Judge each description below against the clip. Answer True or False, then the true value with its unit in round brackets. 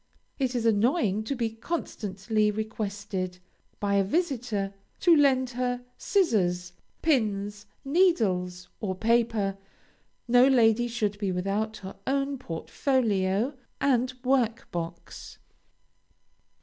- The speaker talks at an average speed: False (105 wpm)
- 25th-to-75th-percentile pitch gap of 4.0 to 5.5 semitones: True (4.4 semitones)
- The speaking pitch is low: False (220 Hz)